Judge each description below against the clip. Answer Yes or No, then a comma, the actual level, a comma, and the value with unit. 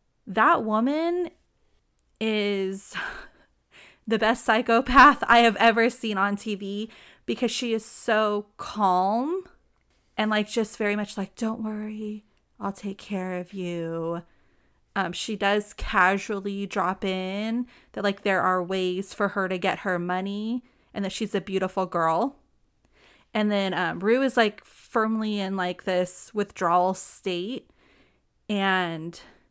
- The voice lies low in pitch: No, high, 205 Hz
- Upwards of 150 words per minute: No, slow, 135 wpm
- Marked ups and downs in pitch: No, average, 2.9 semitones